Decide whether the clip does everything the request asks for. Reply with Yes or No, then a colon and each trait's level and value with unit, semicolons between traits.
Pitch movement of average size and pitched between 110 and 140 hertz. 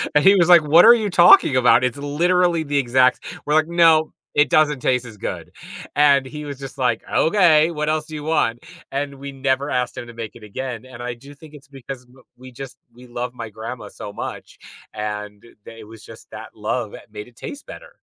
Yes: average, 4.1 semitones; low, 135 Hz